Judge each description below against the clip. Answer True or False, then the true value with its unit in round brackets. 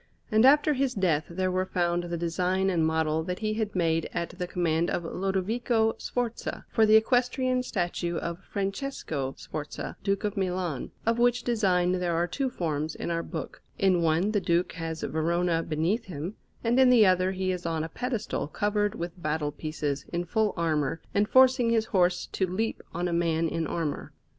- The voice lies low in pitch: False (180 Hz)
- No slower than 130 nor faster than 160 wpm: False (185 wpm)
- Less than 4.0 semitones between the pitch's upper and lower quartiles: False (4.6 semitones)